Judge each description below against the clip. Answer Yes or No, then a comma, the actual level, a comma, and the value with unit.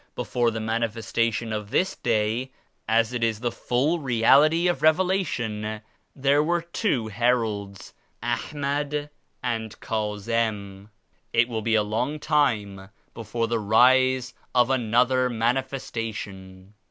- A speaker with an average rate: No, slow, 130 wpm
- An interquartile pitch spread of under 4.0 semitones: Yes, average, 3.4 semitones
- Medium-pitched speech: No, low, 115 Hz